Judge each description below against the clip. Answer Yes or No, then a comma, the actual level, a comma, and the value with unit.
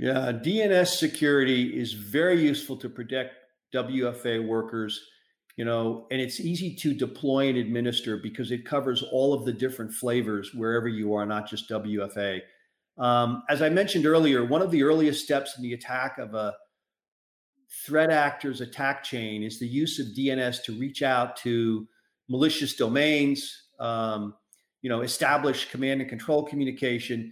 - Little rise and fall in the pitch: No, average, 3.6 semitones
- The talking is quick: No, average, 155 wpm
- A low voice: Yes, low, 130 Hz